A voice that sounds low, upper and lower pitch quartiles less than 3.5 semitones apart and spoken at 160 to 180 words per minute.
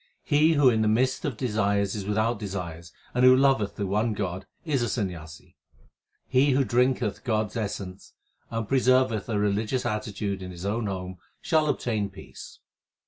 No: low, 110 Hz; average, 4.3 semitones; average, 170 wpm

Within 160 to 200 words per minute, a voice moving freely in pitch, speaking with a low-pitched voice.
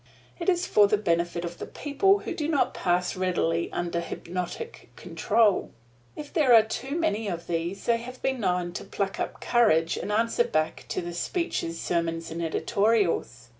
No: average, 175 wpm; wide, 6.0 semitones; high, 195 Hz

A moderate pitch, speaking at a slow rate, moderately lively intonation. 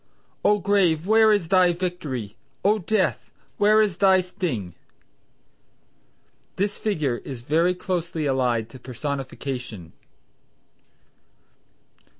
No: medium, 170 Hz; slow, 100 wpm; wide, 7.0 semitones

